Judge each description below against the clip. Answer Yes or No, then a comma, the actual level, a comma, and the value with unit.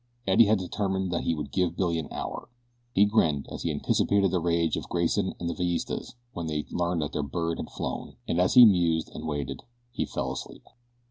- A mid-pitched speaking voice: No, very low, 85 Hz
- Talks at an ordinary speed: No, fast, 210 wpm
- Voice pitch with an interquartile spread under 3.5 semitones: Yes, average, 2.7 semitones